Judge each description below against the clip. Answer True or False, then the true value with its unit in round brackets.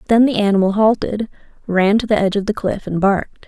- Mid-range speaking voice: False (205 Hz)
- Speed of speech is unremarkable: False (225 wpm)